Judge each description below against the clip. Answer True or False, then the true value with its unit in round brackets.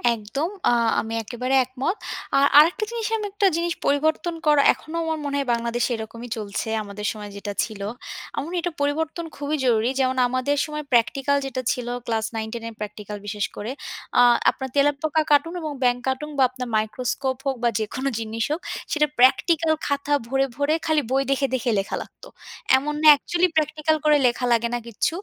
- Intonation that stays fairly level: False (4.6 semitones)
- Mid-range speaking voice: False (270 Hz)